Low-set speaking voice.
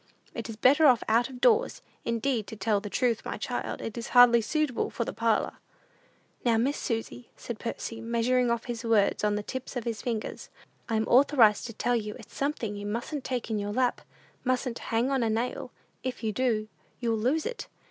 No: high, 235 Hz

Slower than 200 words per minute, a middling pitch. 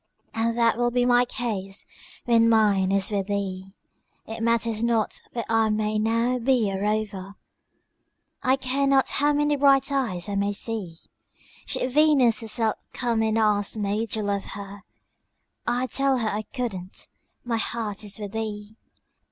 No: average, 160 wpm; high, 225 Hz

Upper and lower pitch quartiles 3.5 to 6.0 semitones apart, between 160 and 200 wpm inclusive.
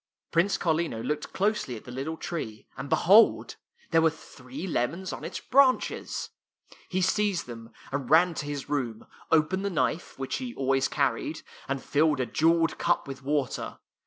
Yes: average, 4.5 semitones; average, 170 wpm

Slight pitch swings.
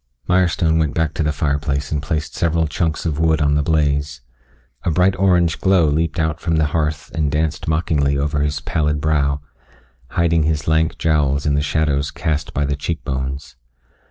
Yes: narrow, 1.9 semitones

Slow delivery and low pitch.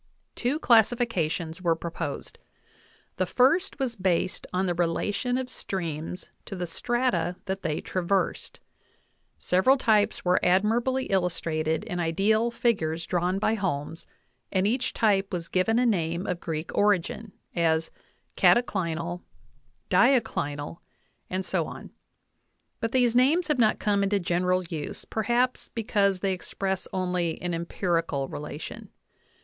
No: slow, 130 wpm; medium, 185 Hz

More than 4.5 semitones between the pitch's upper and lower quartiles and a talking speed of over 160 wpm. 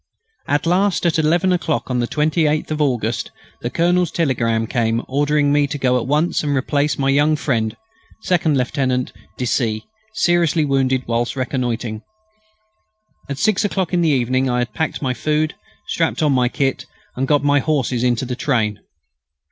No: average, 3.7 semitones; average, 170 wpm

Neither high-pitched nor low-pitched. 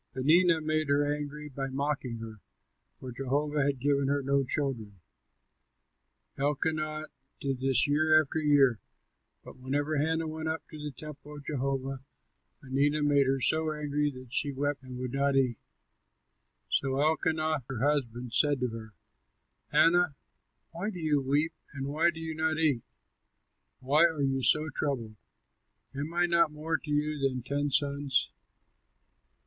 Yes: medium, 145 Hz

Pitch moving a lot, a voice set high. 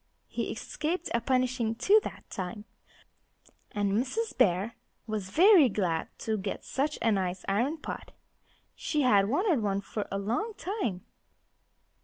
Yes: wide, 7.2 semitones; high, 225 Hz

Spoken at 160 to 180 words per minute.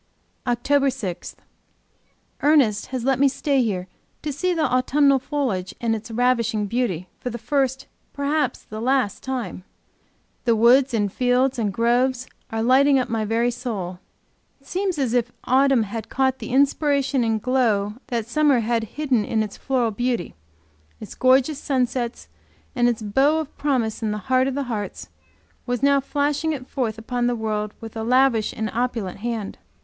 Yes: average, 170 wpm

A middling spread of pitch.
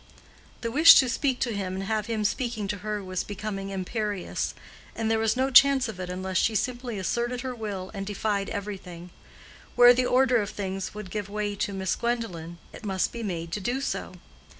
Yes: average, 3.8 semitones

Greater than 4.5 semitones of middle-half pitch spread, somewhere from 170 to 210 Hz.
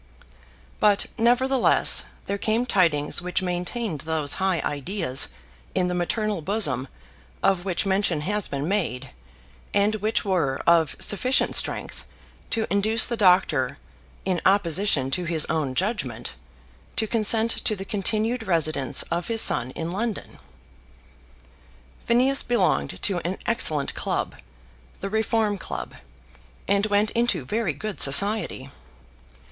Yes: wide, 5.4 semitones; high, 190 Hz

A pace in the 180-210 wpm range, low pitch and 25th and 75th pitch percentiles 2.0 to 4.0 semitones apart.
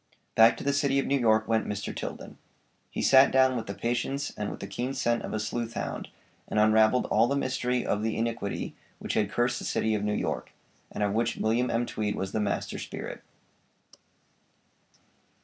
Yes: average, 200 wpm; low, 115 Hz; average, 2.7 semitones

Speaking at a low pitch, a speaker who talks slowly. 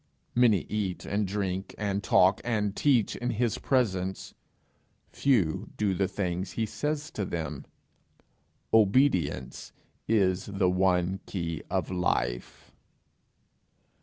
Yes: very low, 95 Hz; slow, 110 wpm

